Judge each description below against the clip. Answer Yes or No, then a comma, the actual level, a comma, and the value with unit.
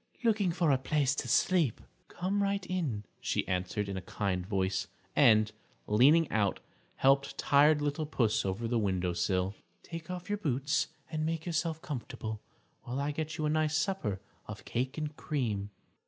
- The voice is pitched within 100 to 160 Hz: Yes, medium, 140 Hz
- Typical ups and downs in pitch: No, wide, 7.1 semitones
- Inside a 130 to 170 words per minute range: Yes, average, 165 wpm